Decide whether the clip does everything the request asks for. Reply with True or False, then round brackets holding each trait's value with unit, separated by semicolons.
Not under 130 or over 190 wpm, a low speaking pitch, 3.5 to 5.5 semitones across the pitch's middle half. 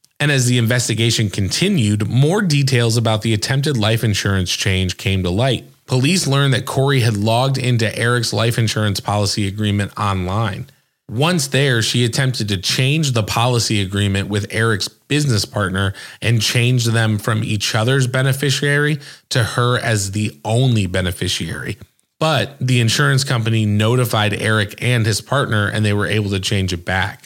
True (160 wpm; 115 Hz; 3.8 semitones)